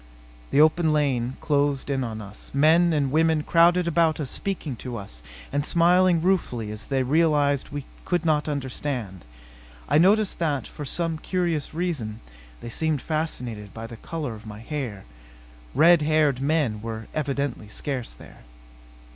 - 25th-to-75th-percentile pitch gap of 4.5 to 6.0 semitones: Yes, average, 4.8 semitones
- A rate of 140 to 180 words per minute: Yes, average, 155 wpm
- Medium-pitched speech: Yes, medium, 145 Hz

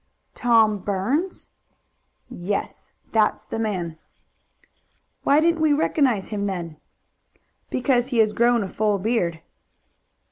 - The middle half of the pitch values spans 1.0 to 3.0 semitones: No, average, 4.3 semitones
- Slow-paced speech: Yes, slow, 110 wpm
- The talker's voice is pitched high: Yes, high, 220 Hz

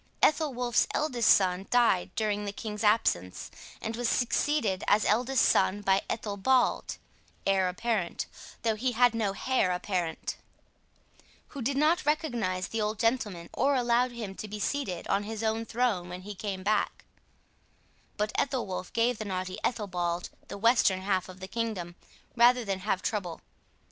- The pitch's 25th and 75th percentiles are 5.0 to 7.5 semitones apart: No, average, 4.2 semitones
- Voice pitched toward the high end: Yes, high, 215 Hz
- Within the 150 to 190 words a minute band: Yes, average, 155 wpm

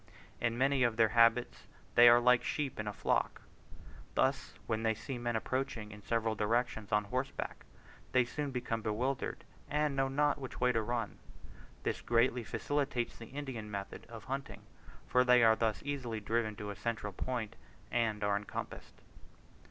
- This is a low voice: Yes, low, 120 Hz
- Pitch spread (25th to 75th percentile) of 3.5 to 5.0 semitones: No, average, 2.7 semitones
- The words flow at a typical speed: Yes, average, 165 wpm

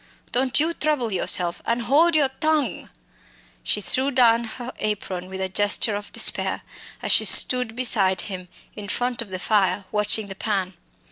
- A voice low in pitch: No, high, 220 Hz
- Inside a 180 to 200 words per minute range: No, average, 165 wpm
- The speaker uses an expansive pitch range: No, average, 4.6 semitones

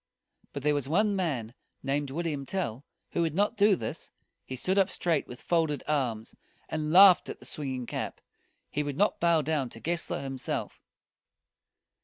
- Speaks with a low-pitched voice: No, medium, 150 Hz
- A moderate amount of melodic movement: Yes, average, 4.3 semitones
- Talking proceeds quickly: No, average, 170 wpm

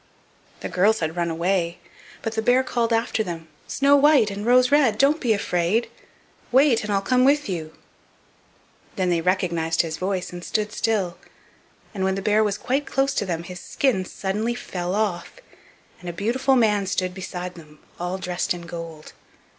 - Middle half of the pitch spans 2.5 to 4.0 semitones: No, average, 4.9 semitones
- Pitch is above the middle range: Yes, high, 195 Hz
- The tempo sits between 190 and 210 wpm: No, average, 180 wpm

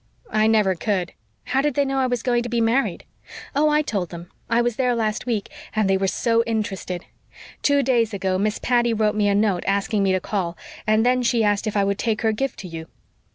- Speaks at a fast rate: Yes, fast, 235 wpm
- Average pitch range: Yes, average, 3.4 semitones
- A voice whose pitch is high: Yes, high, 220 Hz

